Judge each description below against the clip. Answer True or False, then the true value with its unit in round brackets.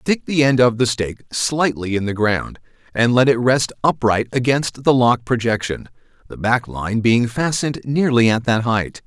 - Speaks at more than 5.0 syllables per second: False (4.6 syllables/s)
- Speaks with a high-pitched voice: False (120 Hz)